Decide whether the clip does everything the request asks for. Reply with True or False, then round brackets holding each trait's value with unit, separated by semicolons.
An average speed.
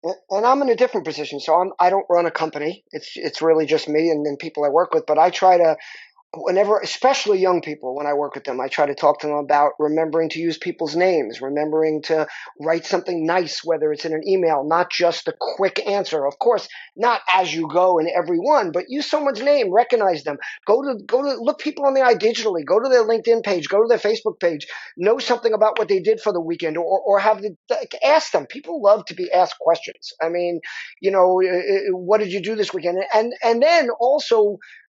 False (230 wpm)